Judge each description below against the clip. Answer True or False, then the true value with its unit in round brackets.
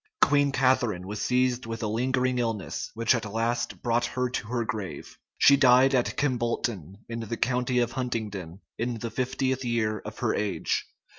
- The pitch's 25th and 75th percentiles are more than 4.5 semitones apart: False (2.5 semitones)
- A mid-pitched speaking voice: False (120 Hz)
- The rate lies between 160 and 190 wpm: True (170 wpm)